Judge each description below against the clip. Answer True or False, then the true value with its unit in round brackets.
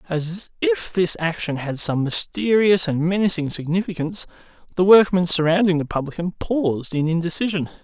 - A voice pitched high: False (170 Hz)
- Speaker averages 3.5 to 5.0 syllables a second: False (5.2 syllables/s)